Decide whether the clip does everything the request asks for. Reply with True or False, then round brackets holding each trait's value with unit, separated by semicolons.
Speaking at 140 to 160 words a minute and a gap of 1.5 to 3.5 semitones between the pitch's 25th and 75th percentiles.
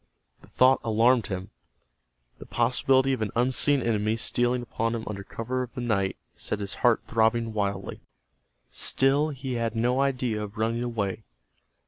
True (155 wpm; 2.7 semitones)